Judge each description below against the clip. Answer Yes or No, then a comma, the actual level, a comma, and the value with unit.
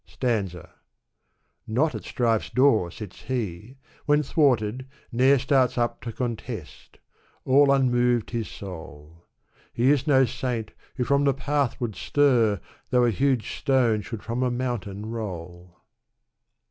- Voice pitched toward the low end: Yes, low, 120 Hz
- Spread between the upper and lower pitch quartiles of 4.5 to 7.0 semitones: No, average, 3.7 semitones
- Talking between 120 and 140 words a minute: Yes, slow, 135 wpm